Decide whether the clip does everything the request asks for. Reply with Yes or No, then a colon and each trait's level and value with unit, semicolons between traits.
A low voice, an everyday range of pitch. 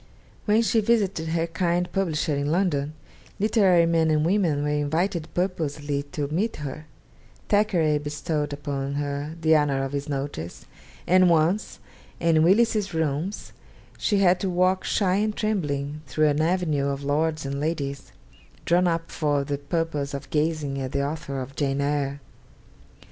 No: medium, 155 Hz; average, 3.9 semitones